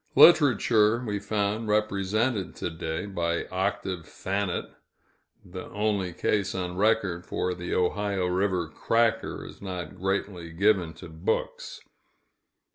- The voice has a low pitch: Yes, very low, 95 Hz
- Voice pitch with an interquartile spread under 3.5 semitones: Yes, average, 2.9 semitones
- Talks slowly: Yes, slow, 120 wpm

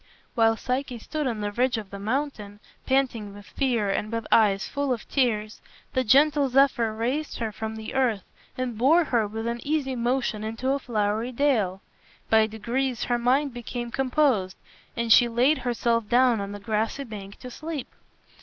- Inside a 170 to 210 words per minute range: Yes, average, 175 wpm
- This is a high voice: Yes, high, 235 Hz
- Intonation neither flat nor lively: Yes, average, 3.4 semitones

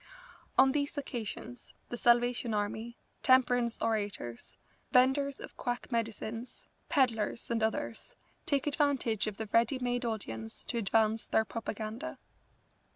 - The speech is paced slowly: Yes, slow, 120 wpm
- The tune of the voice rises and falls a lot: No, average, 2.7 semitones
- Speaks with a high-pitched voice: Yes, high, 235 Hz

